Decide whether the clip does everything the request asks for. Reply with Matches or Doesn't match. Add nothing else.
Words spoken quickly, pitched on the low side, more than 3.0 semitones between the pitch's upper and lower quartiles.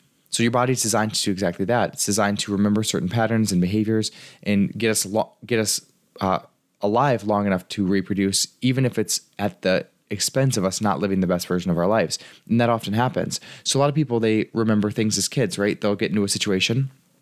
Doesn't match